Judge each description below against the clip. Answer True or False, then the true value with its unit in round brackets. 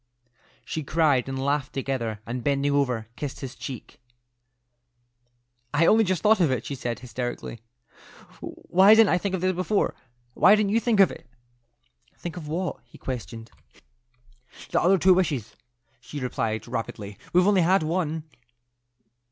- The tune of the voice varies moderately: False (6.7 semitones)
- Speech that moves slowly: False (150 wpm)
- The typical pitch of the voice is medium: True (145 Hz)